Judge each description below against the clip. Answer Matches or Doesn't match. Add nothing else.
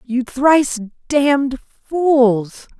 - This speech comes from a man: Doesn't match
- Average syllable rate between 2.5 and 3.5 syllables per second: Matches